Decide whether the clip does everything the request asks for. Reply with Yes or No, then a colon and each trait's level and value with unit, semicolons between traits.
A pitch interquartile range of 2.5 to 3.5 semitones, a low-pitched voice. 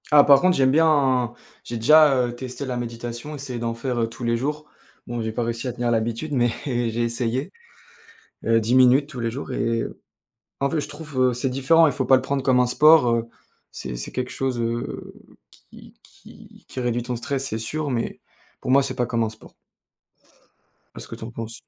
Yes: average, 2.8 semitones; low, 125 Hz